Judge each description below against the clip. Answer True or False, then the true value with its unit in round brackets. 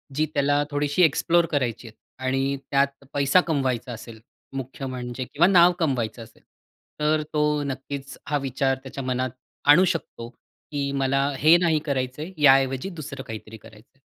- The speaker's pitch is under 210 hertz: True (140 Hz)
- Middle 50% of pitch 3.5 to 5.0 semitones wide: False (2.7 semitones)